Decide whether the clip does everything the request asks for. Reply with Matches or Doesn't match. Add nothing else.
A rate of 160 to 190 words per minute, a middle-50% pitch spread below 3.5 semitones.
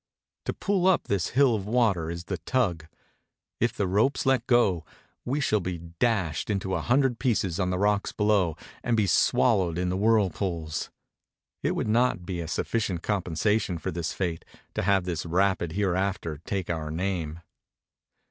Doesn't match